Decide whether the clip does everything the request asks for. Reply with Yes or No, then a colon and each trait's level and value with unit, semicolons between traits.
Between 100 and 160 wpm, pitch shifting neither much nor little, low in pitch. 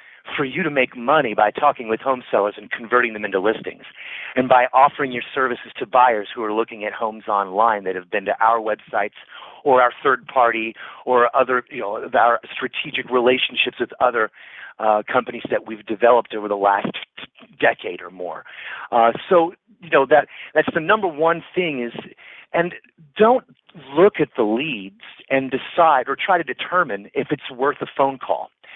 No: average, 180 wpm; average, 4.8 semitones; low, 125 Hz